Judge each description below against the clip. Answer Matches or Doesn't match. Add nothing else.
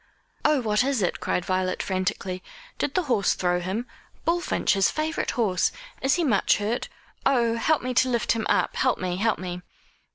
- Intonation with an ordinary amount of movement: Doesn't match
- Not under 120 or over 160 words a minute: Doesn't match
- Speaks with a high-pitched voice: Matches